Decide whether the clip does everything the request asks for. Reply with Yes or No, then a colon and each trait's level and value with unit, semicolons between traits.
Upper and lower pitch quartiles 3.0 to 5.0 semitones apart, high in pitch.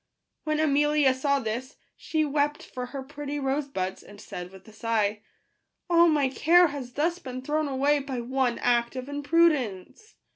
Yes: average, 3.4 semitones; very high, 275 Hz